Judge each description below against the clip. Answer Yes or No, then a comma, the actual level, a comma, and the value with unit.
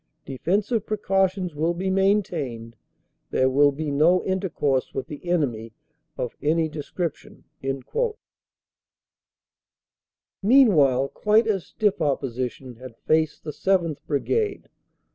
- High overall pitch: No, medium, 160 Hz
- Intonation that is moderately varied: No, wide, 6.0 semitones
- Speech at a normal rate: No, slow, 105 wpm